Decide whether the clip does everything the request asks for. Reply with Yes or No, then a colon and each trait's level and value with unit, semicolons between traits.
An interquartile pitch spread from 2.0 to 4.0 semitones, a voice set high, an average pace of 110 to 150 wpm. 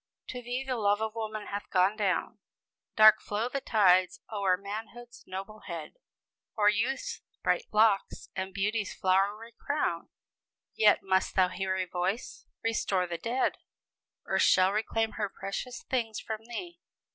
Yes: average, 3.0 semitones; high, 210 Hz; average, 145 wpm